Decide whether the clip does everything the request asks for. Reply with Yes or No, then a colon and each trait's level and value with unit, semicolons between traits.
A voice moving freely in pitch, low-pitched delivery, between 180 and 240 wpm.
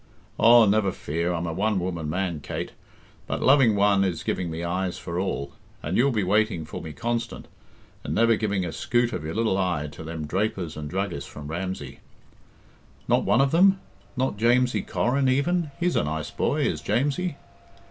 Yes: wide, 6.1 semitones; very low, 95 Hz; average, 190 wpm